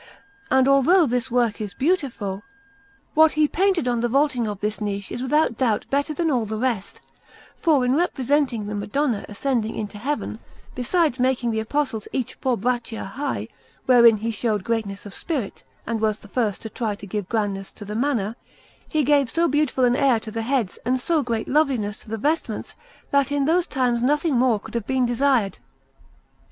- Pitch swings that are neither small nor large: Yes, average, 4.4 semitones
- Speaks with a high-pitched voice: Yes, high, 245 Hz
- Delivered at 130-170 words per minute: No, average, 190 wpm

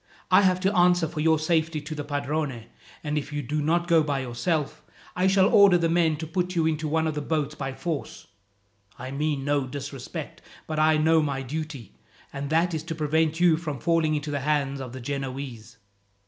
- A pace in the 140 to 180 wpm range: No, fast, 205 wpm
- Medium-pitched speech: Yes, medium, 155 Hz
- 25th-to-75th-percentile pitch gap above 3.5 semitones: No, narrow, 2.5 semitones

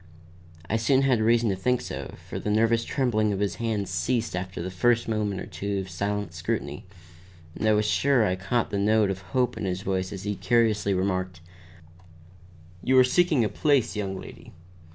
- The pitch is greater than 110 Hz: No, low, 105 Hz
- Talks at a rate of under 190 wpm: No, average, 195 wpm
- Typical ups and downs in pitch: Yes, average, 3.6 semitones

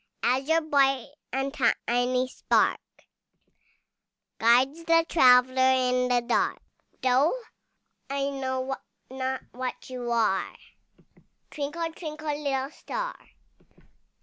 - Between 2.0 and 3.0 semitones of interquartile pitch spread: Yes, narrow, 2.6 semitones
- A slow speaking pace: Yes, slow, 95 wpm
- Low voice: No, very high, 265 Hz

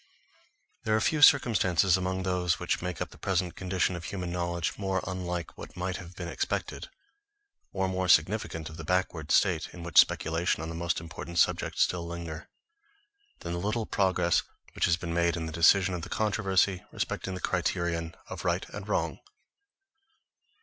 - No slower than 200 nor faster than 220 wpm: No, average, 175 wpm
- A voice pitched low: Yes, very low, 90 Hz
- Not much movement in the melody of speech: Yes, narrow, 1.8 semitones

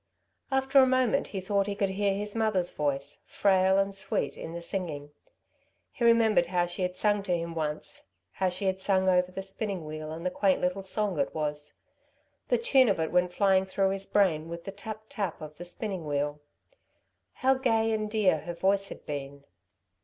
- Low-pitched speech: No, high, 190 Hz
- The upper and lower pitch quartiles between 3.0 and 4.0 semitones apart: Yes, average, 3.6 semitones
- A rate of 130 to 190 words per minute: No, average, 200 wpm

